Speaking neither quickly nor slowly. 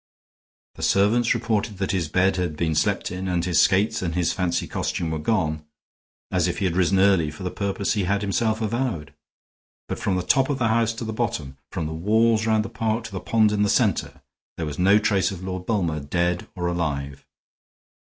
No: fast, 210 wpm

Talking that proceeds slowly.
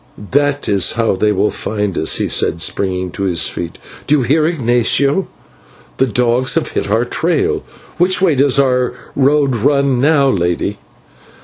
No: average, 165 wpm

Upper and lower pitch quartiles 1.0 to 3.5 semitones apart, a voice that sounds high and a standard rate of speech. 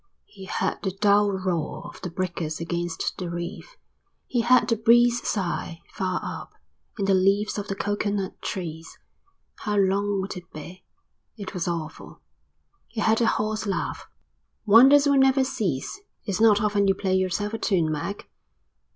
Yes: average, 3.1 semitones; high, 200 Hz; average, 160 wpm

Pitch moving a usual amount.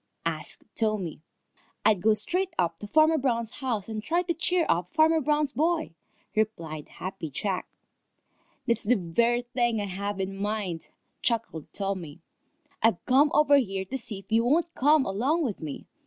No: wide, 6.8 semitones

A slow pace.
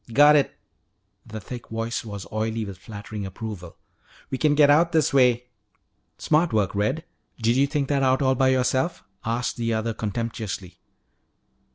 No: average, 165 wpm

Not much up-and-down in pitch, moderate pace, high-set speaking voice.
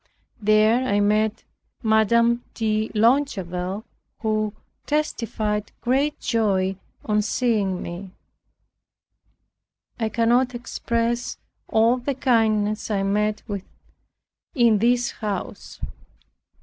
No: narrow, 2.3 semitones; slow, 90 wpm; high, 220 Hz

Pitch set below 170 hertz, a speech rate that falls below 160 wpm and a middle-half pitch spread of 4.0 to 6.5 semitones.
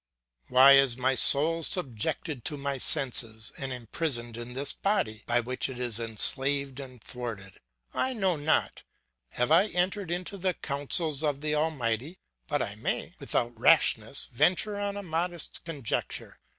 Yes: medium, 140 Hz; average, 150 wpm; average, 5.3 semitones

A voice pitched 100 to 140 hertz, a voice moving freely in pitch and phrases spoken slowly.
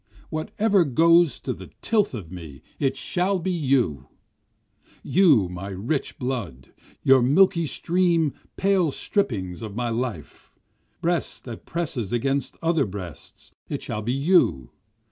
Yes: low, 135 Hz; wide, 8.5 semitones; slow, 130 wpm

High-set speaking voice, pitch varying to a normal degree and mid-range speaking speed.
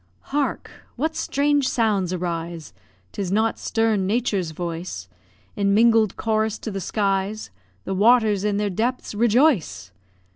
No: high, 210 Hz; average, 3.6 semitones; slow, 125 wpm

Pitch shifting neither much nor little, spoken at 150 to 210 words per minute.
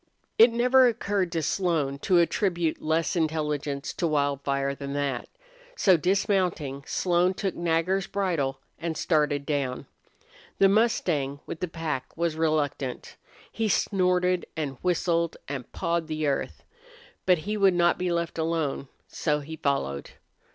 No: average, 4.1 semitones; slow, 135 wpm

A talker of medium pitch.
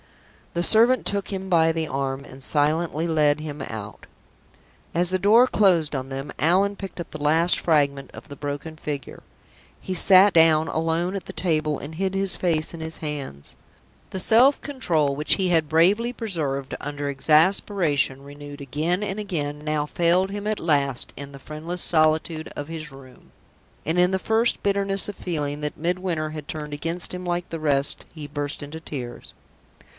Yes: medium, 160 Hz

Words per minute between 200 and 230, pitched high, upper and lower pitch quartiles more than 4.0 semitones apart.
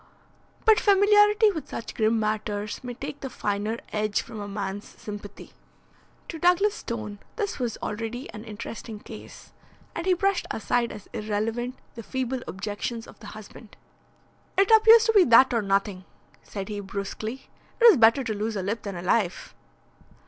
No: average, 165 wpm; high, 225 Hz; average, 5.3 semitones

